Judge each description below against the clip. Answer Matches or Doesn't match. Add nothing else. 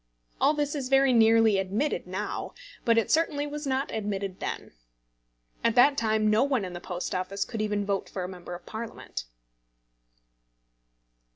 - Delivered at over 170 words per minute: Doesn't match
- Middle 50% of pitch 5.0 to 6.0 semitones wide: Matches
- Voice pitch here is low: Doesn't match